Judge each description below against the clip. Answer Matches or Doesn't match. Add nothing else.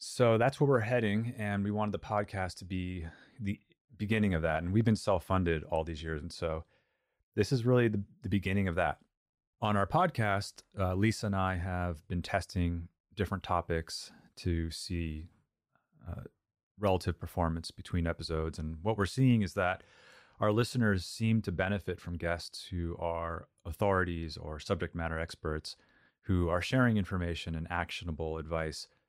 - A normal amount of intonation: Matches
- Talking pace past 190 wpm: Doesn't match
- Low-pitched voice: Matches